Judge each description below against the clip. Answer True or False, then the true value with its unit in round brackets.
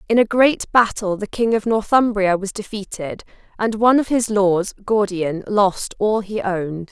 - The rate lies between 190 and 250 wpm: False (175 wpm)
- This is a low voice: False (205 Hz)